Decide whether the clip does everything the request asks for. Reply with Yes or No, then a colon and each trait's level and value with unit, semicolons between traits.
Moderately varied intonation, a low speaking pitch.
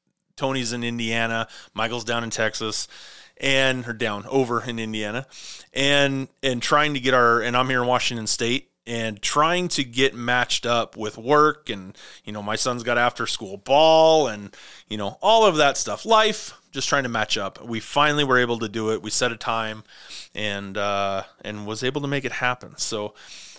Yes: average, 3.6 semitones; low, 120 Hz